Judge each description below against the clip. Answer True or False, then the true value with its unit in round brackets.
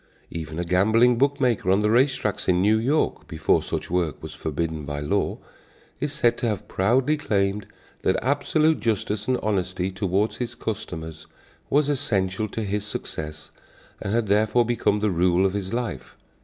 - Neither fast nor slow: True (170 wpm)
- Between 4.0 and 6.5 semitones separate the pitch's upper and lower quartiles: True (4.7 semitones)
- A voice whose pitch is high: False (105 Hz)